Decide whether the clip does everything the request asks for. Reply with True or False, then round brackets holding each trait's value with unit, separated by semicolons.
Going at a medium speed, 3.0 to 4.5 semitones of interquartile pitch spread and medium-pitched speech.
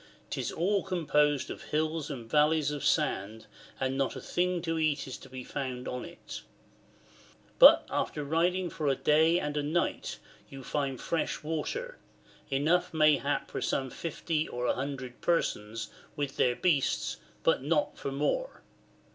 True (155 wpm; 3.4 semitones; 150 Hz)